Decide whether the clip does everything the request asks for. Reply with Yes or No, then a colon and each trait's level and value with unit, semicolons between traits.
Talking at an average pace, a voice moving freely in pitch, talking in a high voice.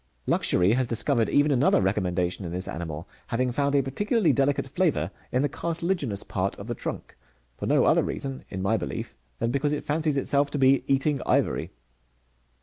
No: average, 180 wpm; wide, 6.2 semitones; low, 135 Hz